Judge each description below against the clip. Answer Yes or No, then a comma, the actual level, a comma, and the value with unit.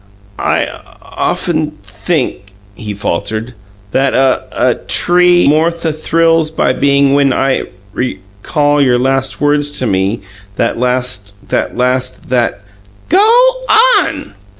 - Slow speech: Yes, slow, 125 wpm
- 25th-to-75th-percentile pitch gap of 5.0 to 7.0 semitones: Yes, wide, 5.4 semitones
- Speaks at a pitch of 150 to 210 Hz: No, low, 135 Hz